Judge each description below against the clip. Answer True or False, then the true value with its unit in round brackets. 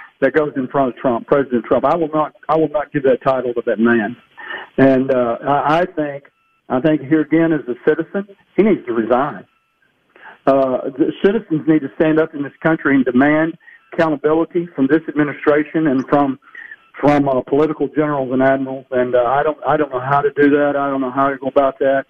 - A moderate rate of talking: False (210 wpm)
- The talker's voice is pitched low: False (145 Hz)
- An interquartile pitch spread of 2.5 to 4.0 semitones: True (2.8 semitones)